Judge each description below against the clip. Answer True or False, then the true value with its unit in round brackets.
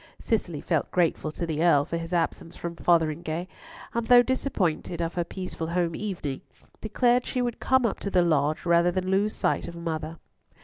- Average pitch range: True (3.4 semitones)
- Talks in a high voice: False (170 Hz)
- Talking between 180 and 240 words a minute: True (185 wpm)